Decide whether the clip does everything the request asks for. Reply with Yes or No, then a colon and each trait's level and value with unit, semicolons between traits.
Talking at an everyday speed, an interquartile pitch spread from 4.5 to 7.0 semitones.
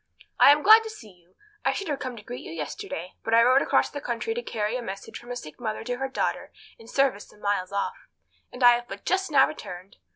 No: fast, 250 wpm; average, 5.1 semitones